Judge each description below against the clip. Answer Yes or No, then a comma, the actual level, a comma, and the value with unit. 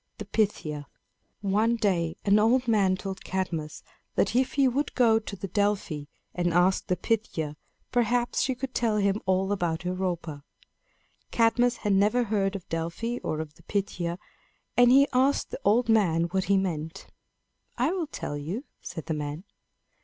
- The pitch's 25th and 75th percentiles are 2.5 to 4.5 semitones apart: No, average, 5.1 semitones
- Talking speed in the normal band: Yes, average, 160 wpm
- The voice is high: Yes, high, 200 Hz